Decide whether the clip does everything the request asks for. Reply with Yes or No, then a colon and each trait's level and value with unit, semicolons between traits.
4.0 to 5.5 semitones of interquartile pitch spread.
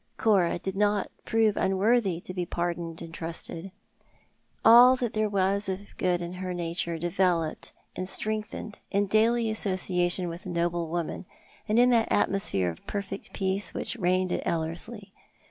No: average, 3.3 semitones